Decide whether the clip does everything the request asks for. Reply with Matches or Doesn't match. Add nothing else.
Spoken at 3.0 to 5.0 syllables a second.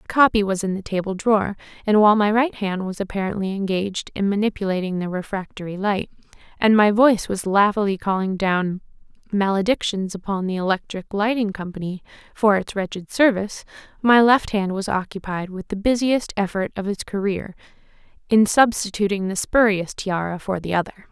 Doesn't match